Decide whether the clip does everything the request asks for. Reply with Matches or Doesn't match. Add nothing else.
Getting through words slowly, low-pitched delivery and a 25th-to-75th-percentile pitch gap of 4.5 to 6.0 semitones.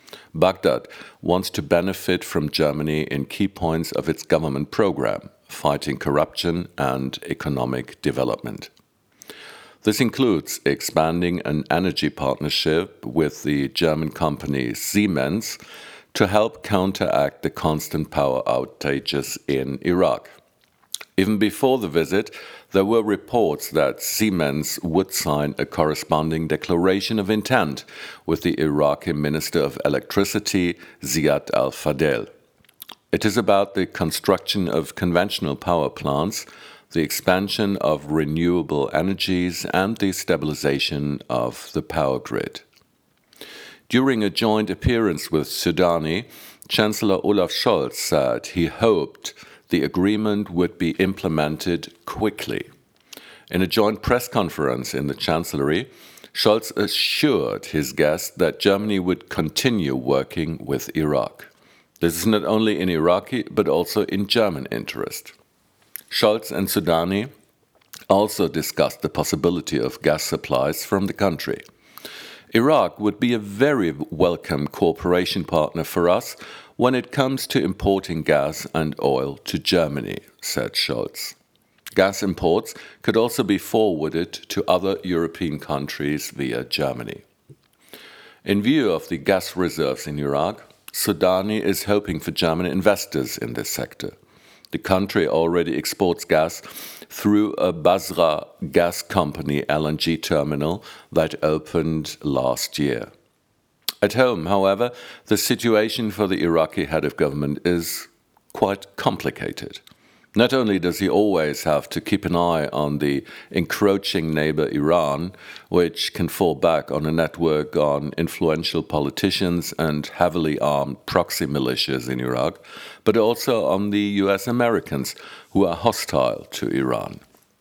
Matches